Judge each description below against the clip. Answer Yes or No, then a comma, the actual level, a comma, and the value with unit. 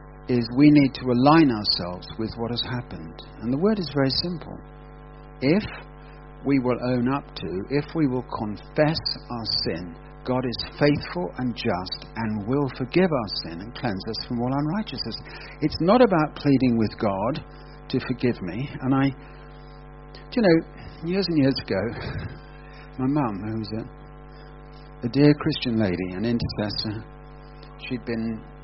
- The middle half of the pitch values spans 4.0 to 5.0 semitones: Yes, average, 4.7 semitones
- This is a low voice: Yes, low, 125 Hz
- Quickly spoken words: No, average, 155 wpm